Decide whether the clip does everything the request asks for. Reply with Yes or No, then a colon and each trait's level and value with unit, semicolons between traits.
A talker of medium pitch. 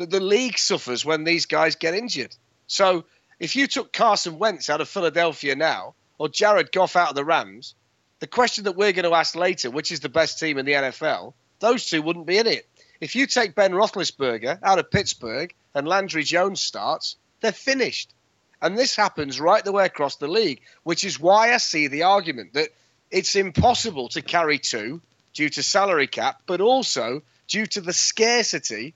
Yes: medium, 170 Hz